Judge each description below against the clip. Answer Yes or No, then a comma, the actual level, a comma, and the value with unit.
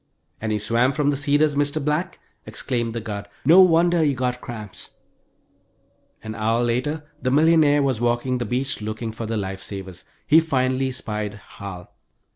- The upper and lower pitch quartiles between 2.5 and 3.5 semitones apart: No, average, 5.0 semitones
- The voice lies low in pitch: Yes, low, 125 Hz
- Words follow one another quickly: No, average, 165 wpm